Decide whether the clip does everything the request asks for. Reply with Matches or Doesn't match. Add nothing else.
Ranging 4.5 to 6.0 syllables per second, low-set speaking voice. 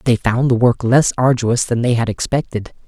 Matches